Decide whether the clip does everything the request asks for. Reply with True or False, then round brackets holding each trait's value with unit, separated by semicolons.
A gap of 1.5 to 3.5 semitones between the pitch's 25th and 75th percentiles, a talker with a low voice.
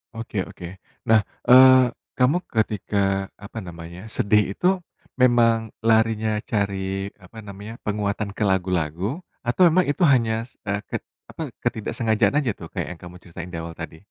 False (4.2 semitones; 105 Hz)